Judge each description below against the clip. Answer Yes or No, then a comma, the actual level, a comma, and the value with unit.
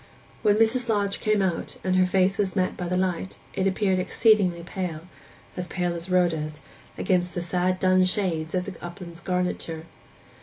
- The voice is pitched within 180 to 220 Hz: Yes, medium, 185 Hz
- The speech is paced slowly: No, average, 160 wpm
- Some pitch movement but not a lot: No, narrow, 1.8 semitones